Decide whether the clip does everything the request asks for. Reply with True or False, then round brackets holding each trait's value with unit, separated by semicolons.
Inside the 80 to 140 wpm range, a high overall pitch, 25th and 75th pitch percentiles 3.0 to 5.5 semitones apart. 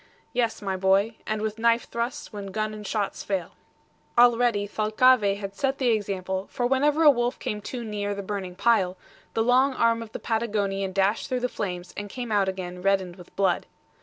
False (195 wpm; 210 Hz; 3.4 semitones)